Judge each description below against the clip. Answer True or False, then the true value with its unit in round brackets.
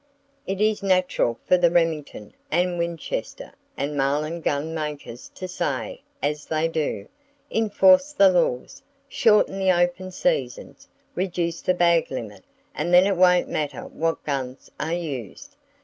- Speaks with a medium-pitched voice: True (170 Hz)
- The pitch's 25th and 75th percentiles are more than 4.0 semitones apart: False (3.7 semitones)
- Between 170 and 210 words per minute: False (140 wpm)